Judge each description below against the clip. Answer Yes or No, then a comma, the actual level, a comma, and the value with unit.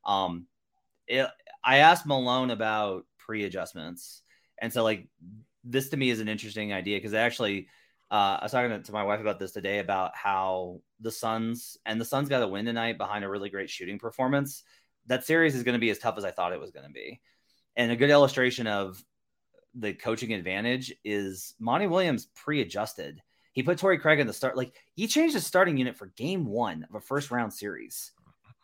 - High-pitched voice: No, low, 115 Hz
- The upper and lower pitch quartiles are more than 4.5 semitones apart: No, average, 4.2 semitones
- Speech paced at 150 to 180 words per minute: No, average, 200 wpm